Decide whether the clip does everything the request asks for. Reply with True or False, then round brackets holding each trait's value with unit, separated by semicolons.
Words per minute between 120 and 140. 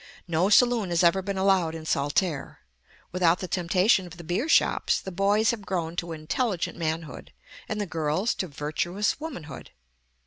False (165 wpm)